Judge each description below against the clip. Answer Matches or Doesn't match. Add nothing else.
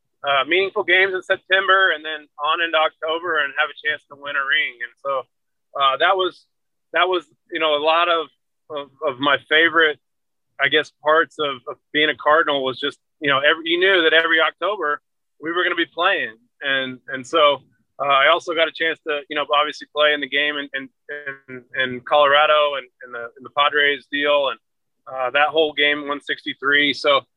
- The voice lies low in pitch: Doesn't match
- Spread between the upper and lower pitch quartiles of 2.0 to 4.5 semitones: Matches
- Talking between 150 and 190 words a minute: Doesn't match